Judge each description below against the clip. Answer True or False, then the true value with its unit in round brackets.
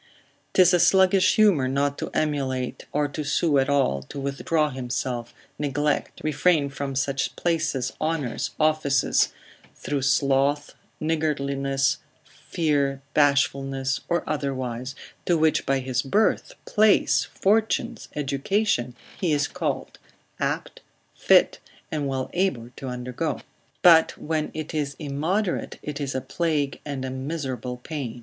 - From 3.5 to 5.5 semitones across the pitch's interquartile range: False (2.8 semitones)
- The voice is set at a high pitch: False (140 Hz)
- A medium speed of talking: False (130 wpm)